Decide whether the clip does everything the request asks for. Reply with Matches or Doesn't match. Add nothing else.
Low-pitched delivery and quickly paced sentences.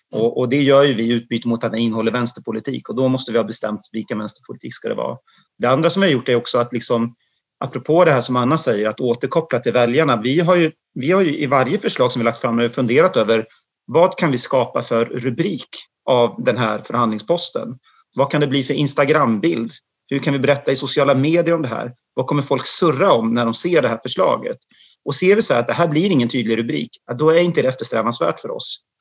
Matches